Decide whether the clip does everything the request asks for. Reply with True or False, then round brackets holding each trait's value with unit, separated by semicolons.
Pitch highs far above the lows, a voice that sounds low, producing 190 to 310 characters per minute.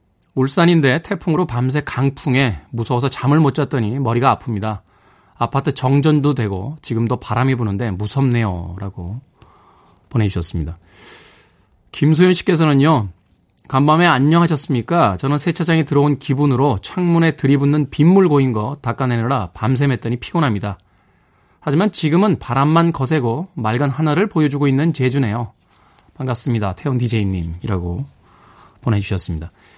False (5.7 semitones; 130 Hz; 335 characters per minute)